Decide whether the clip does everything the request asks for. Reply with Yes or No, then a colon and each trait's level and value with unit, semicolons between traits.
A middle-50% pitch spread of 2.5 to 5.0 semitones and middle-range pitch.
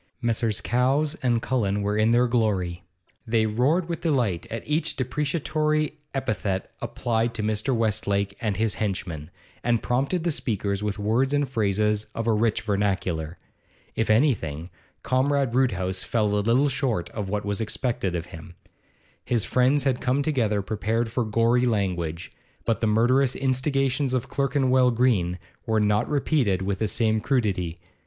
No: average, 4.2 semitones; low, 115 Hz